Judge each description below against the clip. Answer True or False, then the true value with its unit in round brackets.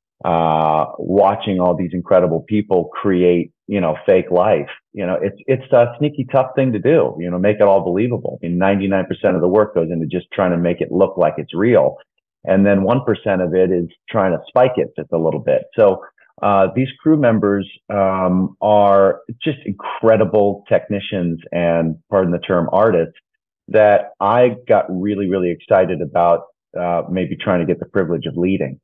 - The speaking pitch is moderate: False (95 Hz)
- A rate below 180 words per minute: False (190 wpm)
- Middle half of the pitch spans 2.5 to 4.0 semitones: True (2.9 semitones)